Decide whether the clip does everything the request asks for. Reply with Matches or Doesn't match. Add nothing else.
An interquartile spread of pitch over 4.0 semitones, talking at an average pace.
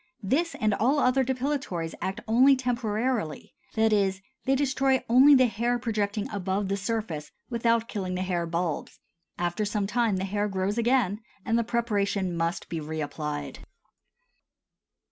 Matches